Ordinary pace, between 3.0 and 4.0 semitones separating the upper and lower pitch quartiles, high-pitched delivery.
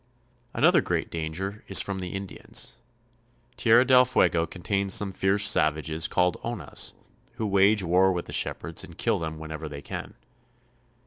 No: average, 150 wpm; average, 3.7 semitones; very low, 95 Hz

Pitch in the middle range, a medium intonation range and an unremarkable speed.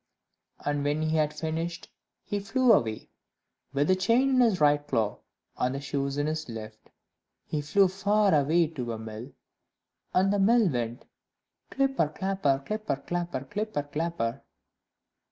No: medium, 155 Hz; wide, 6.0 semitones; average, 150 wpm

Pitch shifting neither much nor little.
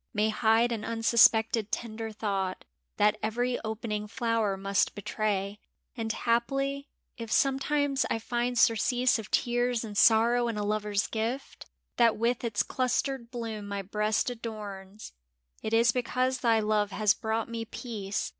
No: narrow, 2.2 semitones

